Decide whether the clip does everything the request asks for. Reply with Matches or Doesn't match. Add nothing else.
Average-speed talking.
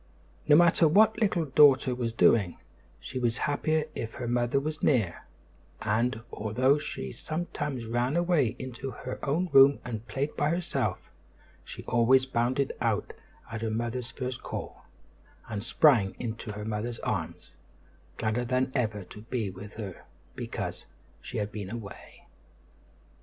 Matches